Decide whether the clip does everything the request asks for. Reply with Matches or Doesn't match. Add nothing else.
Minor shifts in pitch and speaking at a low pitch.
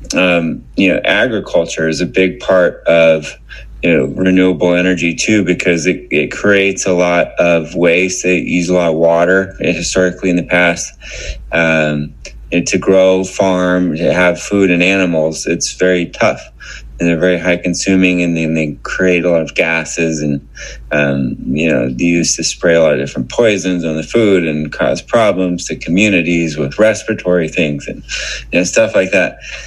Matches